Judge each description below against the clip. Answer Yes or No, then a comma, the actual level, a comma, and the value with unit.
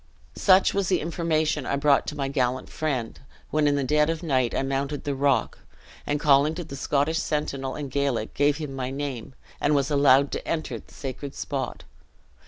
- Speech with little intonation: Yes, narrow, 2.0 semitones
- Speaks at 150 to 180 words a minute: No, average, 190 wpm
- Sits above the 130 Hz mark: Yes, medium, 140 Hz